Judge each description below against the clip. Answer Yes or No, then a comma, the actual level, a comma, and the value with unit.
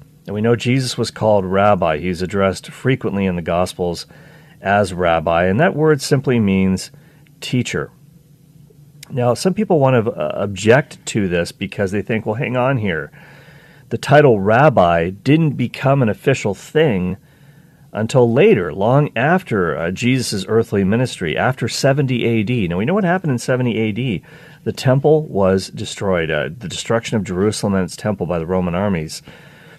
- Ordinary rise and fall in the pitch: No, wide, 6.9 semitones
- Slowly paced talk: No, average, 160 wpm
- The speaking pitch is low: Yes, low, 120 Hz